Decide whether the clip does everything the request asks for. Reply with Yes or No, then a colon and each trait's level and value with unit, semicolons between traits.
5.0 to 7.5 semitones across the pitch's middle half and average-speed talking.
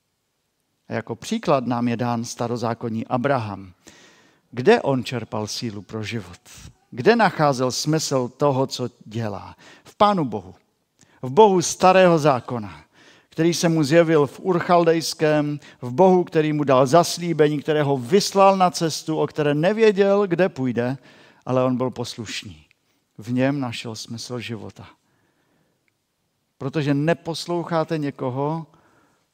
Yes: wide, 5.5 semitones; average, 125 wpm